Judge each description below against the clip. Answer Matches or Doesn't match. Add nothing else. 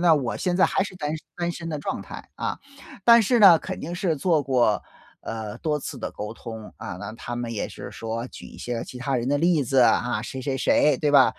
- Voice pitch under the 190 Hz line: Matches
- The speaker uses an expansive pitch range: Matches